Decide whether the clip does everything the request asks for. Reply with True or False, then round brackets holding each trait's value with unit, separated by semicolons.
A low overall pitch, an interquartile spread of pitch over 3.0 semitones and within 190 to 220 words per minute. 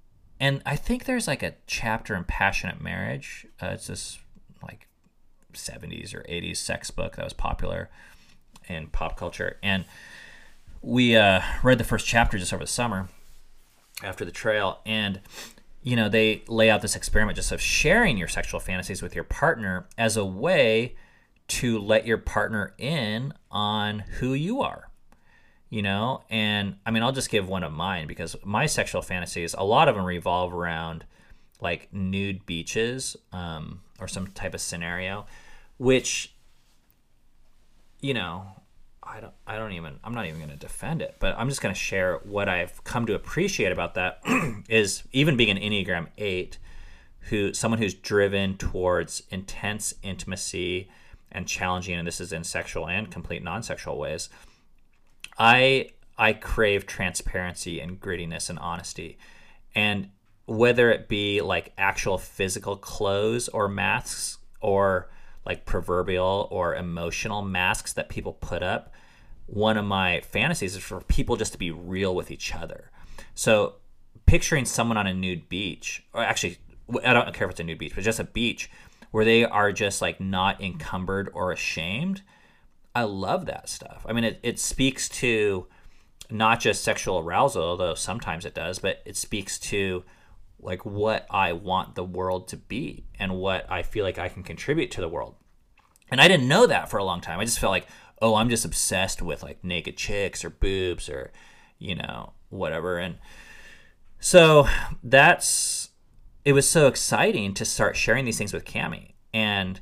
False (100 Hz; 3.7 semitones; 165 wpm)